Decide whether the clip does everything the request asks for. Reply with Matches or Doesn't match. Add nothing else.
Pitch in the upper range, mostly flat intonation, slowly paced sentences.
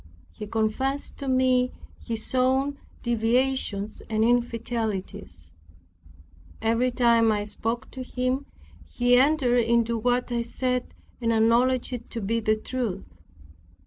Matches